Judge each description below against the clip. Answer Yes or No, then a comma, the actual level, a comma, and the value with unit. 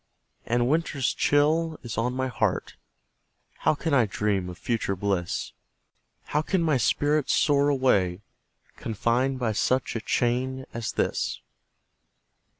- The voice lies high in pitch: No, low, 125 Hz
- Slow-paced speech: Yes, slow, 130 wpm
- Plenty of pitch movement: No, average, 4.6 semitones